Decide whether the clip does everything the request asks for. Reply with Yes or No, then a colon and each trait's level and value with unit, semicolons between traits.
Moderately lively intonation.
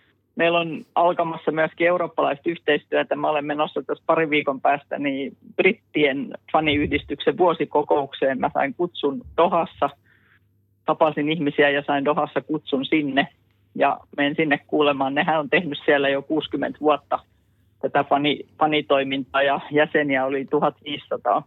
No: narrow, 2.2 semitones